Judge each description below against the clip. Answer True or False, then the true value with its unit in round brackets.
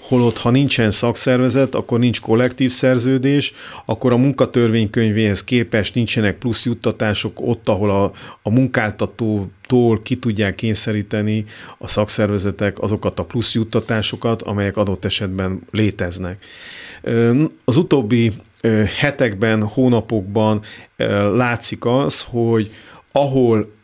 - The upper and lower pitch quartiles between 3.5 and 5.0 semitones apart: False (2.9 semitones)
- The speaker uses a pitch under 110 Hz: False (115 Hz)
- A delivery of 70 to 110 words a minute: True (105 wpm)